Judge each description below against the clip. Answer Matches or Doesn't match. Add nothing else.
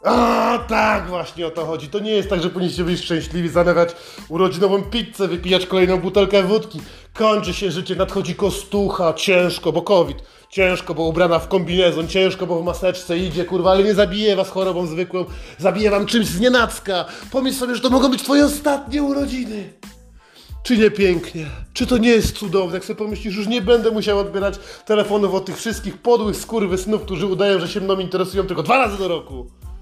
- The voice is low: Doesn't match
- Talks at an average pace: Doesn't match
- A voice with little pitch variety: Doesn't match